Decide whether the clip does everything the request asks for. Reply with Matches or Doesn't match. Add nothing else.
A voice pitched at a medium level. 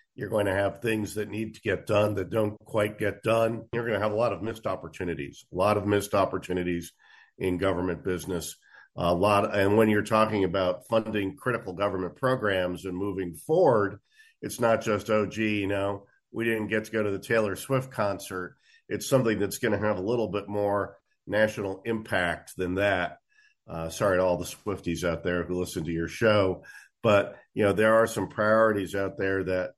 Doesn't match